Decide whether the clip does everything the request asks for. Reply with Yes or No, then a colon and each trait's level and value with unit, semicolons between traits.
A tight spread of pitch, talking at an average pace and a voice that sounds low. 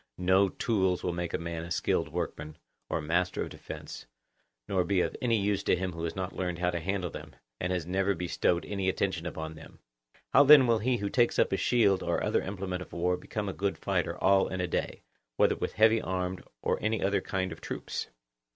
No: narrow, 2.1 semitones; fast, 220 wpm; very low, 95 Hz